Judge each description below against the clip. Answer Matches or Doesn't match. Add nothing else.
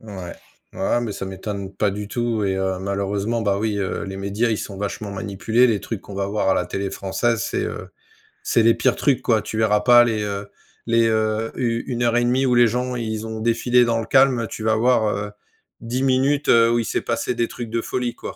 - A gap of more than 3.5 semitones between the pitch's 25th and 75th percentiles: Doesn't match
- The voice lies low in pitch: Matches